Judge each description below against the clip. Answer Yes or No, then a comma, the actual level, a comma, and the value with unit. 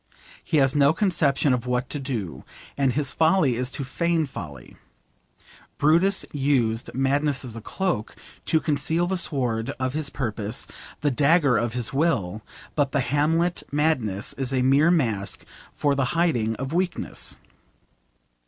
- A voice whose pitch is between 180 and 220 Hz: No, medium, 140 Hz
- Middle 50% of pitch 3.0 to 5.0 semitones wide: Yes, average, 4.3 semitones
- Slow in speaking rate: No, average, 150 wpm